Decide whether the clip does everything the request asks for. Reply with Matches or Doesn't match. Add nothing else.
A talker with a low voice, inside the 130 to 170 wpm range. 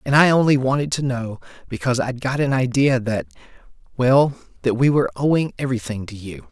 Matches